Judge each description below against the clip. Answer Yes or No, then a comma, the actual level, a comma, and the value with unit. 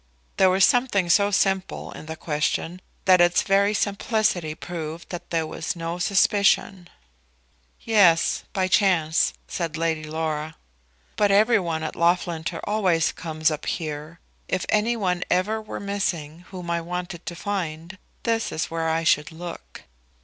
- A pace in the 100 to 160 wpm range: Yes, average, 150 wpm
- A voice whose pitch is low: No, medium, 175 Hz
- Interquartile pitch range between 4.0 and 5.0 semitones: No, average, 3.4 semitones